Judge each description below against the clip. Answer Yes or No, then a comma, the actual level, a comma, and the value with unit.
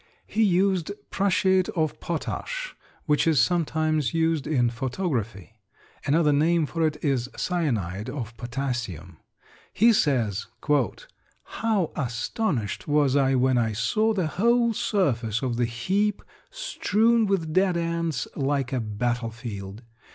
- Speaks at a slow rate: Yes, slow, 125 wpm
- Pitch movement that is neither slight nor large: No, wide, 7.4 semitones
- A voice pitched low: No, medium, 150 Hz